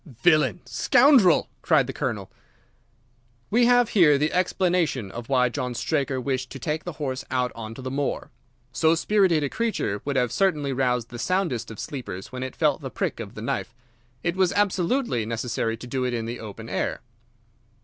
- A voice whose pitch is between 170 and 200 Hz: No, low, 135 Hz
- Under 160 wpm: No, average, 185 wpm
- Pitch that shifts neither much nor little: No, wide, 6.3 semitones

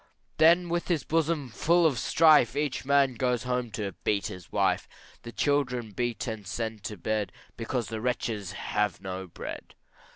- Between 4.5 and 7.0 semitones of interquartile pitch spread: Yes, average, 5.2 semitones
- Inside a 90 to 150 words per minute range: No, average, 165 wpm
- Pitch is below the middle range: Yes, low, 120 Hz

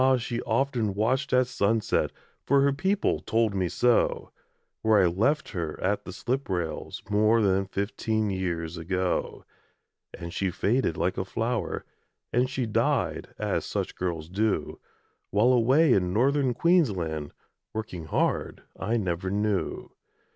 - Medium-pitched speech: No, low, 105 Hz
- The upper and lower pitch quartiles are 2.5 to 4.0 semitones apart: No, average, 5.1 semitones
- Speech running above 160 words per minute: No, average, 140 wpm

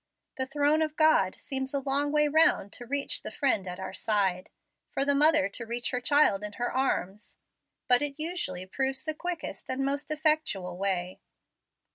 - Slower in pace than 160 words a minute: No, average, 180 wpm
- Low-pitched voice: No, very high, 270 Hz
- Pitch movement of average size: No, wide, 6.5 semitones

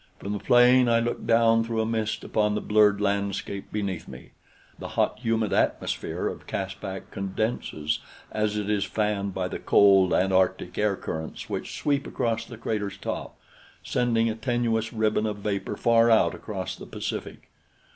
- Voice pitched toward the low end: Yes, low, 105 Hz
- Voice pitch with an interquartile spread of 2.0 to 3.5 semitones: Yes, narrow, 2.4 semitones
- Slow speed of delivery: No, average, 165 wpm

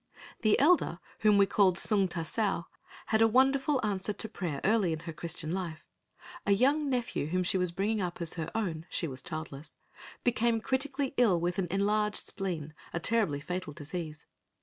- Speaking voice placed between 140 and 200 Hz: Yes, high, 190 Hz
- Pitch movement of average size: Yes, average, 5.0 semitones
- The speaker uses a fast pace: No, average, 175 wpm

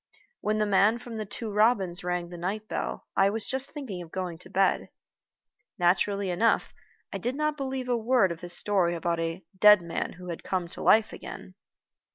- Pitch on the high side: Yes, high, 200 Hz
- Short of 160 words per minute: No, average, 200 wpm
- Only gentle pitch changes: No, average, 4.3 semitones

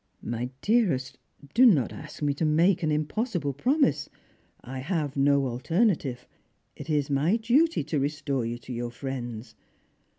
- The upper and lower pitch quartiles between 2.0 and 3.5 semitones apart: No, average, 5.2 semitones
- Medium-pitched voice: Yes, medium, 145 Hz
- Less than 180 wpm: Yes, average, 155 wpm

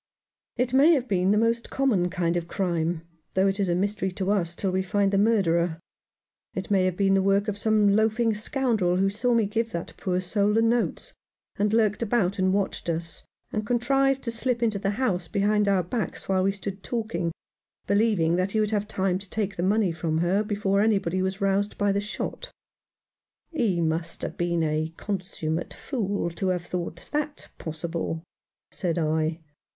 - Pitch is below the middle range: No, high, 195 Hz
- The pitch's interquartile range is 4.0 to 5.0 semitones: No, average, 3.5 semitones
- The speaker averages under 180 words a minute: No, average, 190 wpm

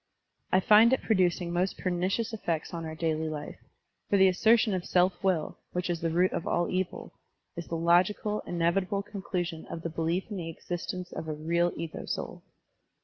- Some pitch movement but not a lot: No, narrow, 2.3 semitones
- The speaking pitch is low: No, medium, 175 Hz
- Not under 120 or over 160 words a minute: No, average, 185 wpm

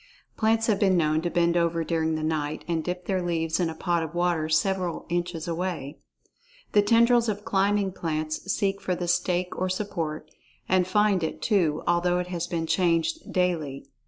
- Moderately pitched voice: Yes, medium, 175 Hz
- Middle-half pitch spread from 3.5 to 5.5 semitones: No, average, 2.8 semitones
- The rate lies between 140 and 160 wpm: No, average, 185 wpm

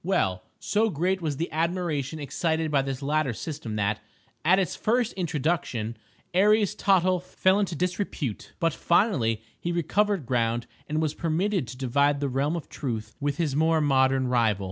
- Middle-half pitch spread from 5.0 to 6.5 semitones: Yes, wide, 5.5 semitones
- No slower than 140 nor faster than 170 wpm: Yes, average, 165 wpm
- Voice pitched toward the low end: No, medium, 155 Hz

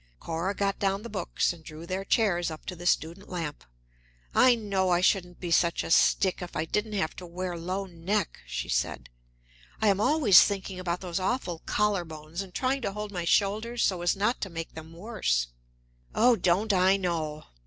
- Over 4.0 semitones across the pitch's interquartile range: No, average, 3.2 semitones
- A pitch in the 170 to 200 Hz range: Yes, medium, 185 Hz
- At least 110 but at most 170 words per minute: No, average, 195 wpm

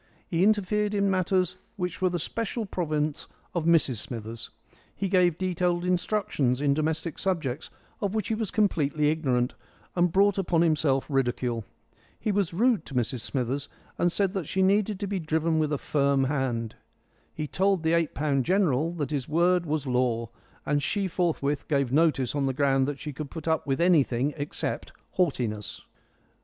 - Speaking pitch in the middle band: Yes, medium, 160 Hz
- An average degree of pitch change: Yes, average, 5.0 semitones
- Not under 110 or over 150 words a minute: No, average, 170 wpm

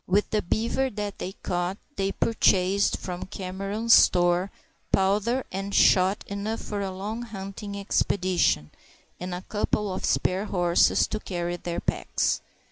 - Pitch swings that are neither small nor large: No, narrow, 2.3 semitones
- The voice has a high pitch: Yes, high, 195 Hz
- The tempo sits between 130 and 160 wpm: Yes, average, 140 wpm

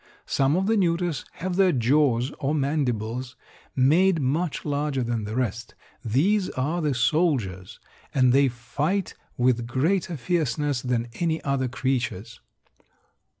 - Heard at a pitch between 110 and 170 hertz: Yes, low, 135 Hz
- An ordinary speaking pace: No, slow, 130 wpm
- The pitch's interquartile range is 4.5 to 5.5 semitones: Yes, average, 5.0 semitones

